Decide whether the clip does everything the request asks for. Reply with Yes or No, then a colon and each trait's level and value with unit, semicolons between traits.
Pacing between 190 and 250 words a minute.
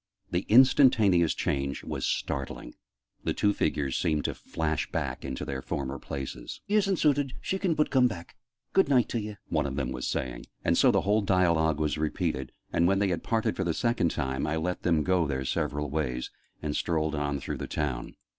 Yes: average, 200 wpm